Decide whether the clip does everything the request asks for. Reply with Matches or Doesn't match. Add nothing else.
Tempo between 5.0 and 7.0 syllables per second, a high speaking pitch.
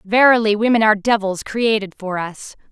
Matches